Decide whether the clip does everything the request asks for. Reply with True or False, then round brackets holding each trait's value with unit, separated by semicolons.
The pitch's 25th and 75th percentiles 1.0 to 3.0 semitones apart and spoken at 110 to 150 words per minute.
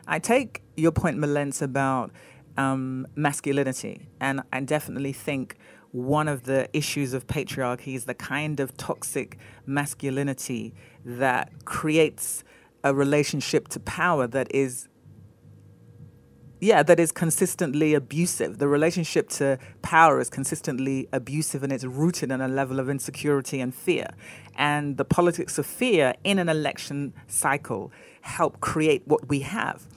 True (2.4 semitones; 135 wpm)